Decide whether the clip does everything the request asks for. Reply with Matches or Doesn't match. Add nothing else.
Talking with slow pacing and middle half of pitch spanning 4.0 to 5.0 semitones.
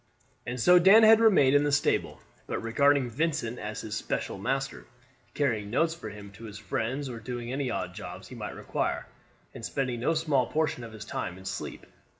Doesn't match